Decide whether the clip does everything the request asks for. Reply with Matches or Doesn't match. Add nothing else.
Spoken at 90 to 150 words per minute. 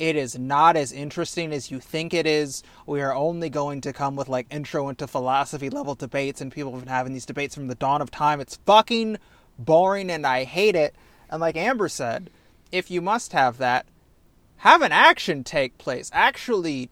Doesn't match